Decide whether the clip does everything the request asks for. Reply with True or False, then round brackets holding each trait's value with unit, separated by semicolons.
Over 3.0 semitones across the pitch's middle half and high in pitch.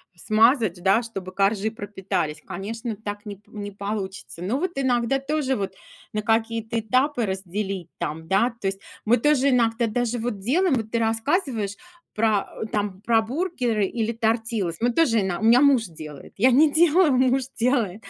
True (3.9 semitones; 225 Hz)